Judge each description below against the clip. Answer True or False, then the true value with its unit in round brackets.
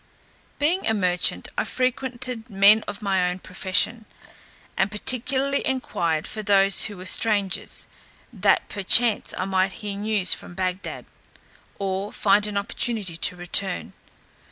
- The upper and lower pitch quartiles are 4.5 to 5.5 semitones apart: False (3.1 semitones)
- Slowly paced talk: True (130 wpm)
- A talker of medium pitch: False (200 Hz)